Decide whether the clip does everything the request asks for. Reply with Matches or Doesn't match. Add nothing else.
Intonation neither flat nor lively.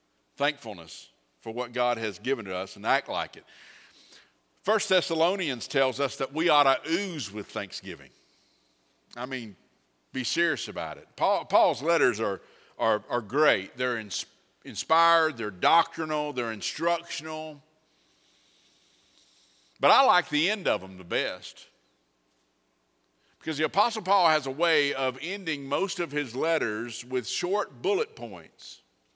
Doesn't match